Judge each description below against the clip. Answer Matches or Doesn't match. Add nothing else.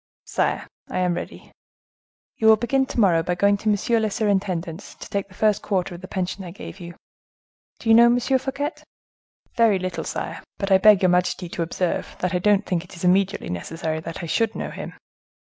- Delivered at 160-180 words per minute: Doesn't match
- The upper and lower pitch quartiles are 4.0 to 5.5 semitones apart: Doesn't match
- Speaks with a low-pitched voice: Doesn't match